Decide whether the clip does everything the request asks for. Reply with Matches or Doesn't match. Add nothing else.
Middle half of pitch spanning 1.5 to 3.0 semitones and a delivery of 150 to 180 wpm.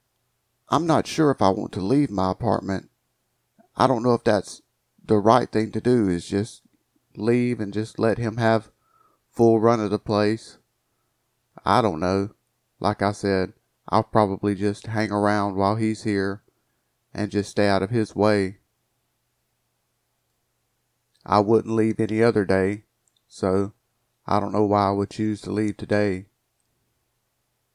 Matches